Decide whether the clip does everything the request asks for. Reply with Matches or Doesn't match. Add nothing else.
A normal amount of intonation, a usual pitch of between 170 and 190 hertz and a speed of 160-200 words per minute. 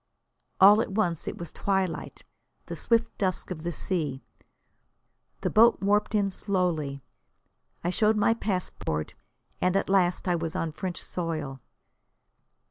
Doesn't match